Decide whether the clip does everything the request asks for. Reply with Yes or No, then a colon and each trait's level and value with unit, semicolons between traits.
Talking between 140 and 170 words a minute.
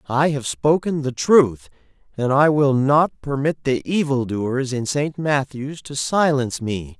Yes: average, 165 wpm